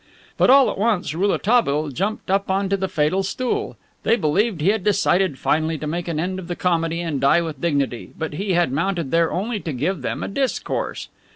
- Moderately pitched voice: Yes, medium, 175 Hz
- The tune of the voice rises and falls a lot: No, average, 4.1 semitones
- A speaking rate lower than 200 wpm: No, fast, 205 wpm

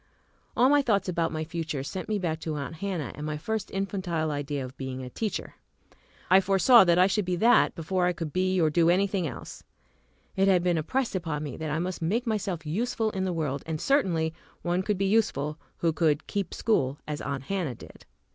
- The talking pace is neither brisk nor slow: No, fast, 215 wpm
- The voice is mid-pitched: Yes, medium, 175 Hz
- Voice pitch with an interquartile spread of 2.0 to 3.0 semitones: No, average, 4.2 semitones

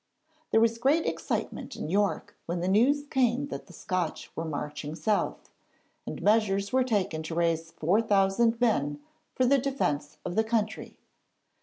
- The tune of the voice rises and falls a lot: Yes, wide, 6.1 semitones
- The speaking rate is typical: Yes, average, 155 wpm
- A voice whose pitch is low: No, high, 200 Hz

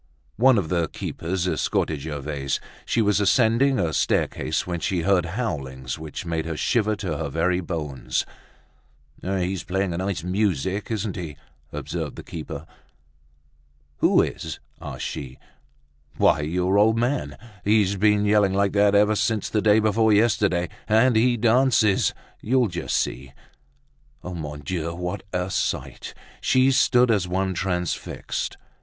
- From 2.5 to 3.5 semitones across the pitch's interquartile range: No, average, 4.4 semitones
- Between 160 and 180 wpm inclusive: No, average, 140 wpm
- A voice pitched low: Yes, very low, 95 Hz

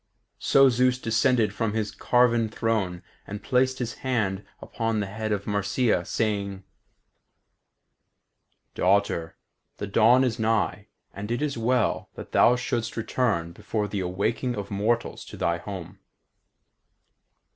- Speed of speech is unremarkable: No, slow, 130 wpm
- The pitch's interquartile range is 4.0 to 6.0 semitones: No, average, 3.1 semitones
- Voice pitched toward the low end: Yes, low, 110 Hz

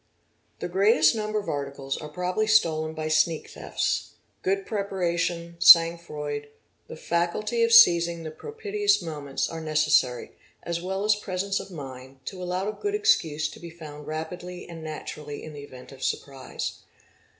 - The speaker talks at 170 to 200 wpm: No, average, 160 wpm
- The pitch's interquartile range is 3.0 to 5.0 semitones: Yes, average, 4.2 semitones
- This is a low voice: No, medium, 170 Hz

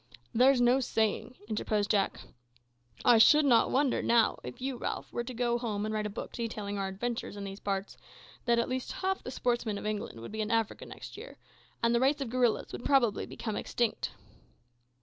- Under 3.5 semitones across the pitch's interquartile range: Yes, average, 2.9 semitones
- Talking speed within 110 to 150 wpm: No, average, 200 wpm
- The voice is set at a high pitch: Yes, high, 235 Hz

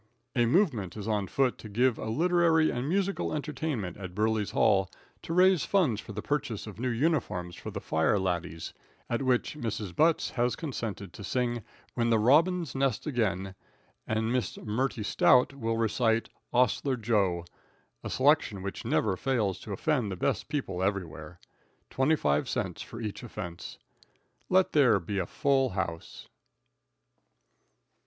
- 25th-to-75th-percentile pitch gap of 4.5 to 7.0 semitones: Yes, wide, 5.6 semitones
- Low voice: Yes, low, 115 Hz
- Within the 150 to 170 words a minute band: Yes, average, 155 wpm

